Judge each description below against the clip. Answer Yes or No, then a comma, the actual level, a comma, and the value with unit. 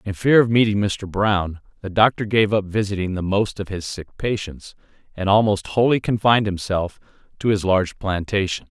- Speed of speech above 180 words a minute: No, average, 175 wpm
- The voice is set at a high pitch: No, low, 100 Hz